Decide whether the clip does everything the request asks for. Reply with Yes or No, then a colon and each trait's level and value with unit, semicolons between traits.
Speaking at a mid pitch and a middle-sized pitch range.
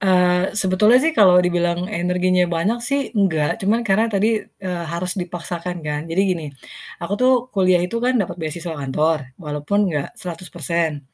Yes: medium, 180 Hz; average, 3.2 semitones